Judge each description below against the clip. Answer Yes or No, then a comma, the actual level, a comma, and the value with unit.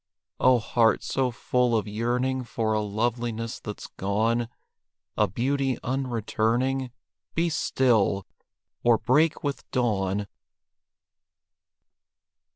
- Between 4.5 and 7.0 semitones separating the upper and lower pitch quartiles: No, average, 2.9 semitones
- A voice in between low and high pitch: No, low, 120 Hz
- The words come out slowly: Yes, slow, 95 wpm